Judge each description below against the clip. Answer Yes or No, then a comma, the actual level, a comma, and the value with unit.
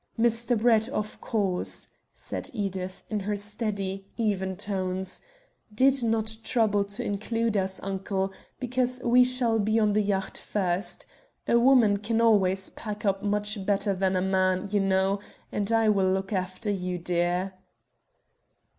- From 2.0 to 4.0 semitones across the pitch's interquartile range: Yes, average, 2.8 semitones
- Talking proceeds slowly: No, average, 145 wpm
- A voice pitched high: Yes, high, 205 Hz